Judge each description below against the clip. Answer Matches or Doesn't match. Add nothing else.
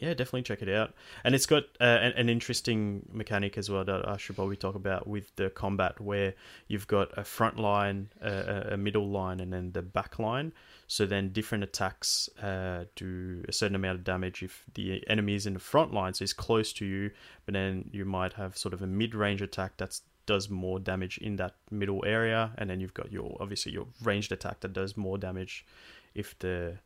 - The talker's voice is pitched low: Matches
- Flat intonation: Matches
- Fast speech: Matches